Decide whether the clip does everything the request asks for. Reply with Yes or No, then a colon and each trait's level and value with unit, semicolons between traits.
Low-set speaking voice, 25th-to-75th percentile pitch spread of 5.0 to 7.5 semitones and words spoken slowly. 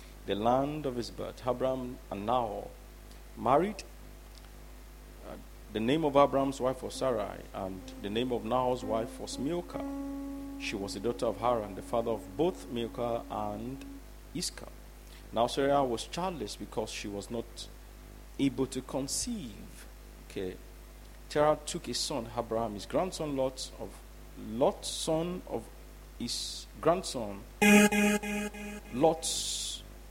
Yes: low, 130 Hz; wide, 5.5 semitones; slow, 130 wpm